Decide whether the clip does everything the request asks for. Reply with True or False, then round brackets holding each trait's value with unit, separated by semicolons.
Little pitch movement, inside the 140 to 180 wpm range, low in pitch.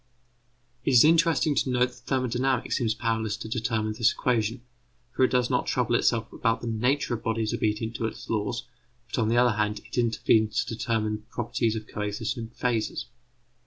False (2.2 semitones; 190 wpm; 115 Hz)